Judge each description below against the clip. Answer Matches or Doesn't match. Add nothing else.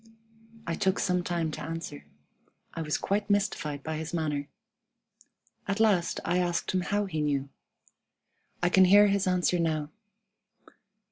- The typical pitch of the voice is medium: Matches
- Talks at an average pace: Matches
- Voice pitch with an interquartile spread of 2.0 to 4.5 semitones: Matches